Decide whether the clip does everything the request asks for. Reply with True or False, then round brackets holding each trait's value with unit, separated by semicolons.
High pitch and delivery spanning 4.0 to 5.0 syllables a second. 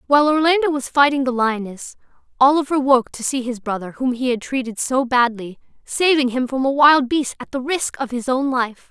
False (260 Hz; 5.2 syllables/s)